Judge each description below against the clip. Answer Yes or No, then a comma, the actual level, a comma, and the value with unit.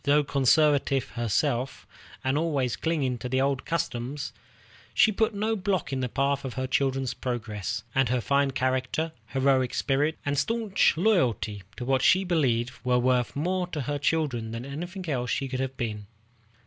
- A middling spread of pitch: Yes, average, 3.8 semitones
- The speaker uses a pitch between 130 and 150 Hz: Yes, low, 135 Hz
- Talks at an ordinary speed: Yes, average, 165 wpm